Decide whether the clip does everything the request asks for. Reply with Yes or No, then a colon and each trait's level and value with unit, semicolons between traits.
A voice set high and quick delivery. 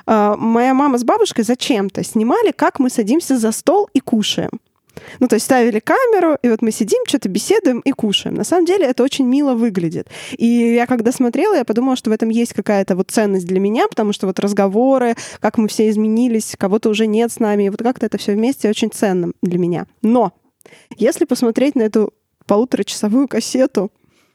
Yes: high, 230 Hz; fast, 190 wpm